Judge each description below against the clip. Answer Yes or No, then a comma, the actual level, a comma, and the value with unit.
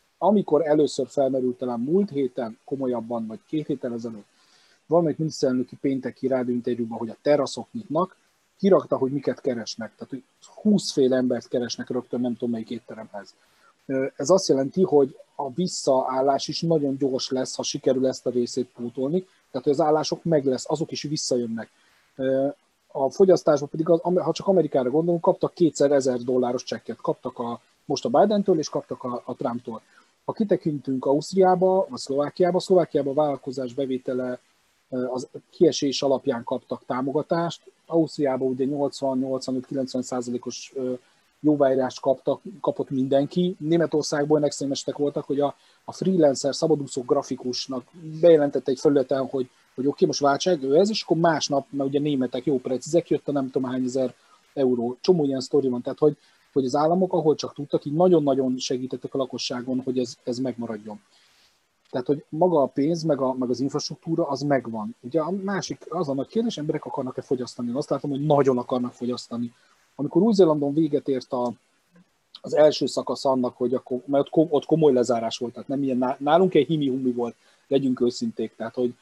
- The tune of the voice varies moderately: Yes, average, 3.4 semitones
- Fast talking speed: Yes, fast, 165 wpm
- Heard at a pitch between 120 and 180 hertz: Yes, low, 135 Hz